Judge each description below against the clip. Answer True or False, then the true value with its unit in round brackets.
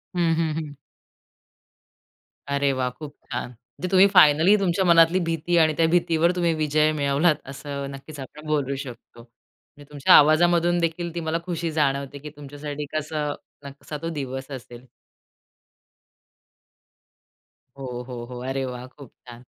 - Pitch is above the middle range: False (150 Hz)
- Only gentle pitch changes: False (3.3 semitones)